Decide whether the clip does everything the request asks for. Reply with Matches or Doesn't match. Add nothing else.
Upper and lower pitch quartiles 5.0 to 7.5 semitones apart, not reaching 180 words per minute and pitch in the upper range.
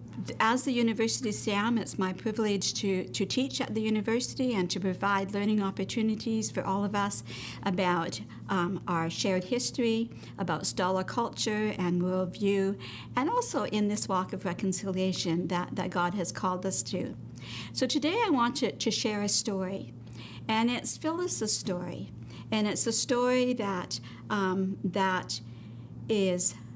Doesn't match